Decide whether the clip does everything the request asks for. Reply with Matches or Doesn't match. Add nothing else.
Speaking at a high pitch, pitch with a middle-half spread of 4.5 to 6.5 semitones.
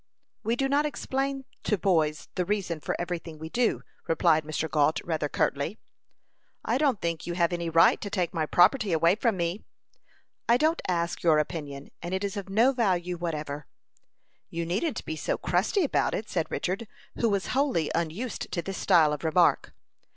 Doesn't match